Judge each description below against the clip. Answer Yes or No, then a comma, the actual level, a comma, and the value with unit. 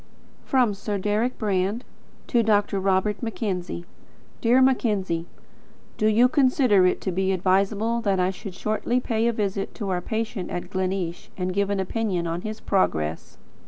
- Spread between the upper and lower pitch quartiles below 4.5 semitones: Yes, average, 3.2 semitones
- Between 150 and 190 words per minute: Yes, average, 160 wpm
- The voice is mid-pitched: No, high, 200 Hz